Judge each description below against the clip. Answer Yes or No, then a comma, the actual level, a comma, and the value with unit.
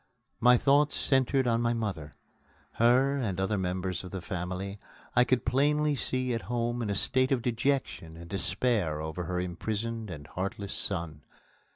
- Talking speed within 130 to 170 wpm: Yes, average, 165 wpm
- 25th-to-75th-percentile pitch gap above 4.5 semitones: Yes, wide, 5.5 semitones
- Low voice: Yes, low, 110 Hz